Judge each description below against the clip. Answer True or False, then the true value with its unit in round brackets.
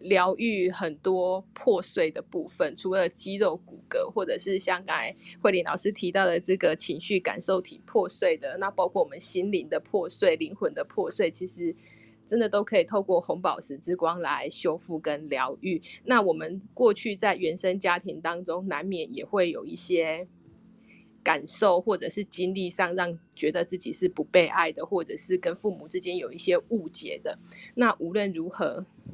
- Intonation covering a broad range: False (4.7 semitones)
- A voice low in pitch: False (185 Hz)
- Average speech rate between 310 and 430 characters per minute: False (265 characters per minute)